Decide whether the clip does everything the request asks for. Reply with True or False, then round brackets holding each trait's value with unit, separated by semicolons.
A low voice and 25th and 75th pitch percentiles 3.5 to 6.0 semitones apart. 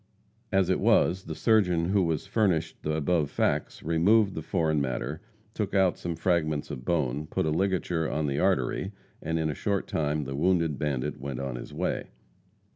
True (80 Hz; 4.1 semitones)